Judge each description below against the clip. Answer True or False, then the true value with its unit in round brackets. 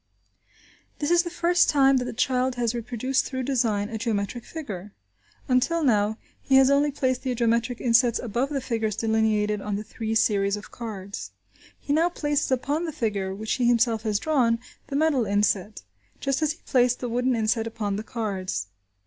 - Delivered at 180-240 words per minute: True (185 wpm)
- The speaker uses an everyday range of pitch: True (3.9 semitones)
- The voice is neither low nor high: False (235 Hz)